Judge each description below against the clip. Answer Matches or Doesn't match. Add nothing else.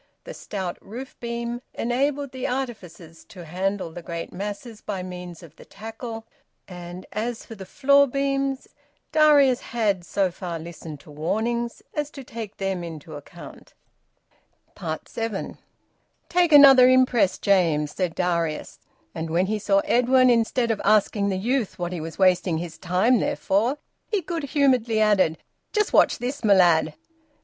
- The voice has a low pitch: Doesn't match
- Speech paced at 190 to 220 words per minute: Doesn't match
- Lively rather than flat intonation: Matches